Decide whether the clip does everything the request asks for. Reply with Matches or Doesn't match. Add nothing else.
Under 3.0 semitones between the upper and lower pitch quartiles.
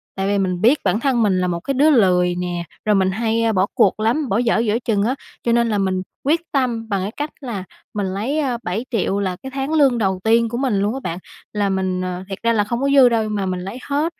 Doesn't match